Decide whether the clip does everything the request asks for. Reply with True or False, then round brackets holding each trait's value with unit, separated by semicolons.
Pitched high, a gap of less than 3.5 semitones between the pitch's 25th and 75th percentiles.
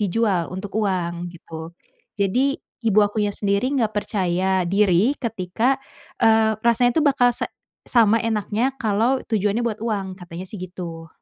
False (205 Hz; 3.8 semitones)